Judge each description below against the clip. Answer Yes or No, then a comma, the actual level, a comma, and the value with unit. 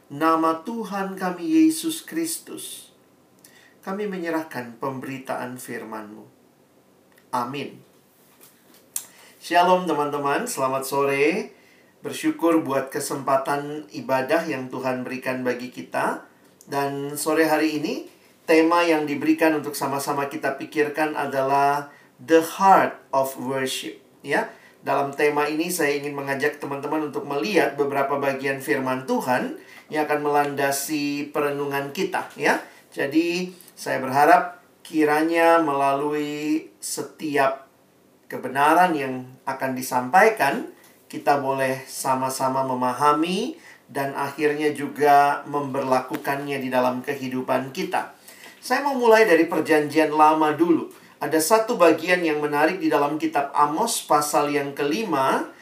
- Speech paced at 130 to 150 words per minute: No, average, 110 wpm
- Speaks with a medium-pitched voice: Yes, medium, 145 Hz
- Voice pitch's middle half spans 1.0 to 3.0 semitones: Yes, average, 2.7 semitones